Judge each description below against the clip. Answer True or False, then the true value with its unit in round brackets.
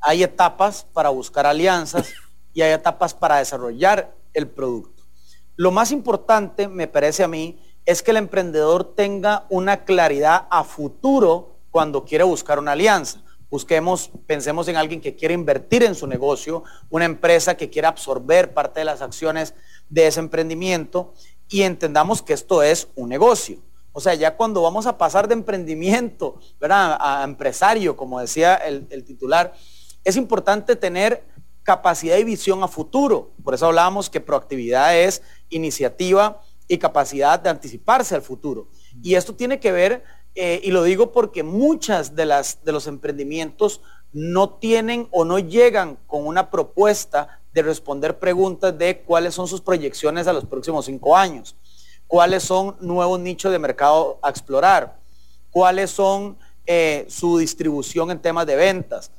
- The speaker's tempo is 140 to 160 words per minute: True (155 wpm)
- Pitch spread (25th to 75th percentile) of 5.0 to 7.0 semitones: False (4.5 semitones)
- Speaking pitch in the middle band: True (170 Hz)